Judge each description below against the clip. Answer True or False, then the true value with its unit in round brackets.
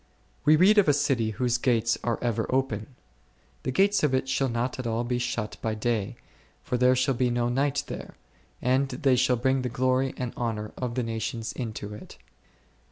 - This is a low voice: True (125 Hz)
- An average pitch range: False (2.2 semitones)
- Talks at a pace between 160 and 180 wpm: False (200 wpm)